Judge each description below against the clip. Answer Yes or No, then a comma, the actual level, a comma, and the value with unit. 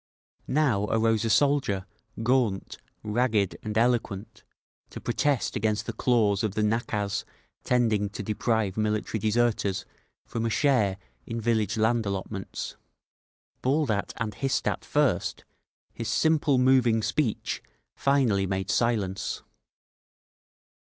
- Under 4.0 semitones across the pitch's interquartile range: Yes, average, 3.1 semitones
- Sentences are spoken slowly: Yes, slow, 120 wpm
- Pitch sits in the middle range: No, low, 110 Hz